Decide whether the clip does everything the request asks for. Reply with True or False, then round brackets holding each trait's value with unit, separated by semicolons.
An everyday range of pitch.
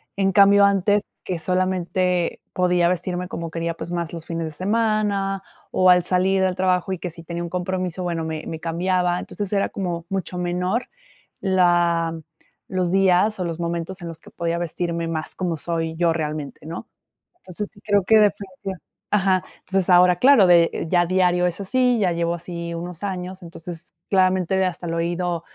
False (2.0 semitones)